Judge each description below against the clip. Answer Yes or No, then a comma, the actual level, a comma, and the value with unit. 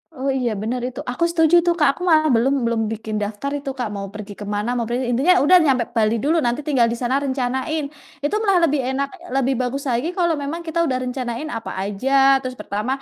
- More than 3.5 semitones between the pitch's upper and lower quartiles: Yes, average, 4.0 semitones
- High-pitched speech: Yes, very high, 255 Hz